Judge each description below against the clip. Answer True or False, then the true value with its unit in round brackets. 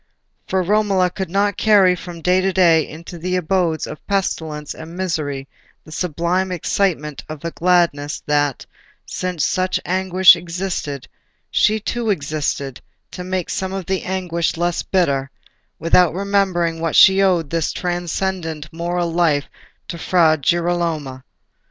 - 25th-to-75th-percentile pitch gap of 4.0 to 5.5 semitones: False (2.9 semitones)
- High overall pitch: False (175 Hz)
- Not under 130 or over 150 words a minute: True (140 wpm)